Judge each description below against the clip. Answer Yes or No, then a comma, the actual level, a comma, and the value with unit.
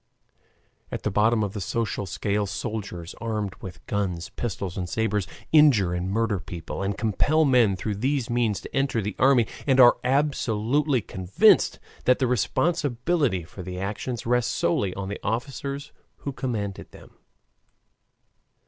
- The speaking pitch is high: No, low, 110 Hz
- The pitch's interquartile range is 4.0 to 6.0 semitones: Yes, average, 4.6 semitones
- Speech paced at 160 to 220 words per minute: No, average, 150 wpm